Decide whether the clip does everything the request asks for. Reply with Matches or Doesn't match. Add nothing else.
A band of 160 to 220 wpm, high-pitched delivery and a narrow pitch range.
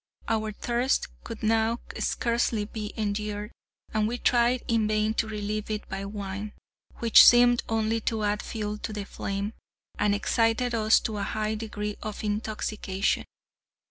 Doesn't match